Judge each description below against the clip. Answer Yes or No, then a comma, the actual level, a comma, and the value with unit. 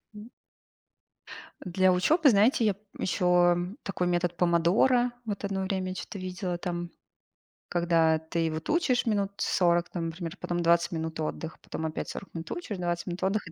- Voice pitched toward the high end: No, medium, 180 Hz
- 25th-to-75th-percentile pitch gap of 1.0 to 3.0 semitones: Yes, average, 2.7 semitones